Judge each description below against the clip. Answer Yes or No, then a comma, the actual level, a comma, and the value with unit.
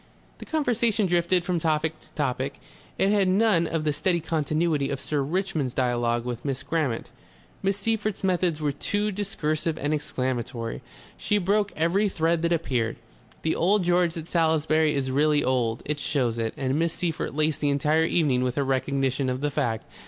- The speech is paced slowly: No, average, 175 wpm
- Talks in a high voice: No, medium, 155 Hz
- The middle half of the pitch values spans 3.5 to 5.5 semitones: Yes, average, 4.5 semitones